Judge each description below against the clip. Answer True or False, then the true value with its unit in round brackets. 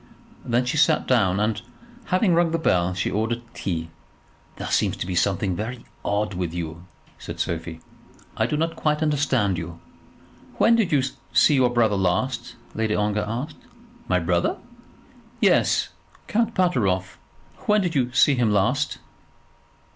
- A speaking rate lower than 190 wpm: True (150 wpm)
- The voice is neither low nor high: False (115 Hz)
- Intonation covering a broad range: True (8.0 semitones)